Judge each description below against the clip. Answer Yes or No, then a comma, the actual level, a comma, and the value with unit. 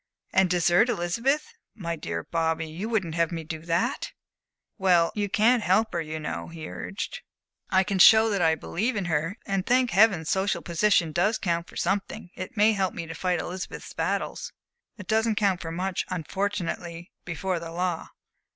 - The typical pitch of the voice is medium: Yes, medium, 180 Hz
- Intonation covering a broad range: No, average, 3.6 semitones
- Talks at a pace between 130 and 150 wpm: No, average, 180 wpm